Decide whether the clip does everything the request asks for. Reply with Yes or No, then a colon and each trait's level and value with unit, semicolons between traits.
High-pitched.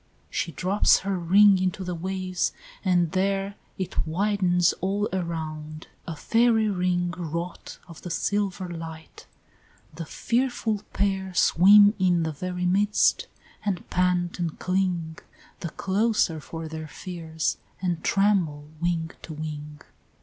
No: medium, 180 Hz